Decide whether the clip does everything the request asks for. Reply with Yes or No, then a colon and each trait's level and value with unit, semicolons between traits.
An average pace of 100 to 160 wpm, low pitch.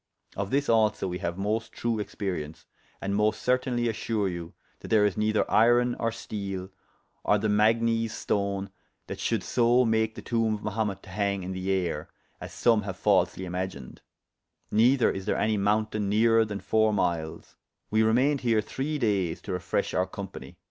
No: average, 175 wpm; low, 105 Hz